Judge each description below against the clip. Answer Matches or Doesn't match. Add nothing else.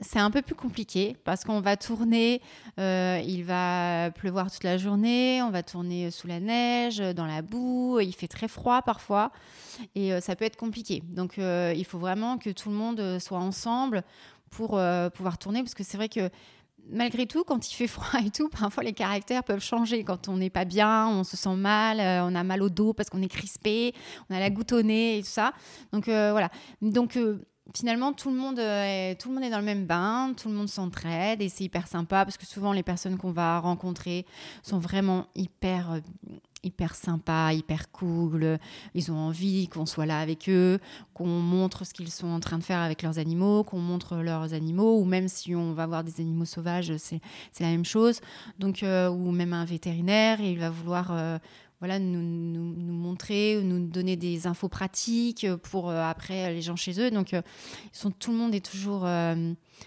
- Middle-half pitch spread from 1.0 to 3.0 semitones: Doesn't match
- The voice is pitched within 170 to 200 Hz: Matches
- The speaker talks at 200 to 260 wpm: Matches